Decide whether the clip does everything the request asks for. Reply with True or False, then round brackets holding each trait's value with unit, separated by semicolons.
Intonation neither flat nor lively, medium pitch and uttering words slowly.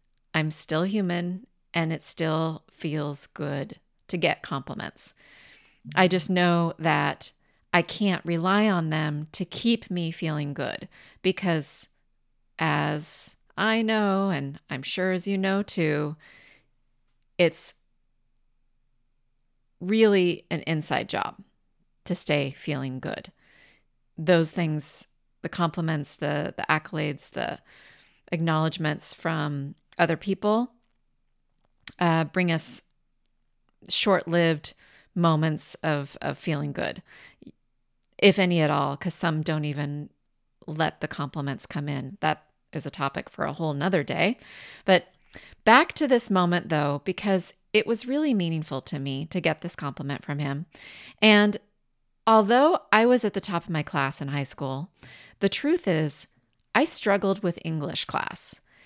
True (4.4 semitones; 160 Hz; 130 wpm)